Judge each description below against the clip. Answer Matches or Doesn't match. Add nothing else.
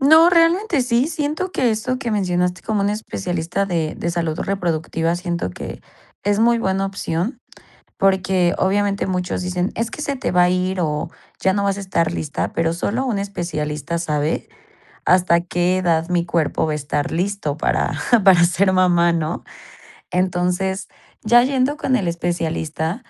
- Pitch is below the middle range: Doesn't match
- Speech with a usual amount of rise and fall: Matches